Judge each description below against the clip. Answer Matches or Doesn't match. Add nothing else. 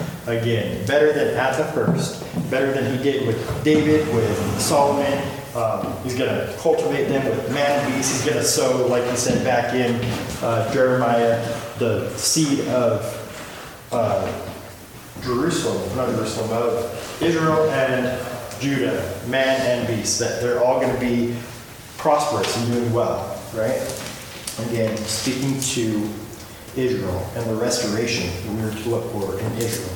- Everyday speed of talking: Matches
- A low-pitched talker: Matches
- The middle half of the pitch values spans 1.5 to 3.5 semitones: Matches